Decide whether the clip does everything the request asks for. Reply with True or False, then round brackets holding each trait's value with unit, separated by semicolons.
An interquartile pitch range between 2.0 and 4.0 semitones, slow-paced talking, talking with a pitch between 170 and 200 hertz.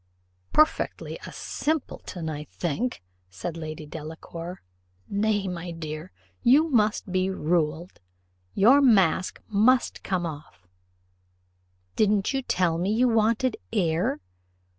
False (5.4 semitones; 110 wpm; 185 Hz)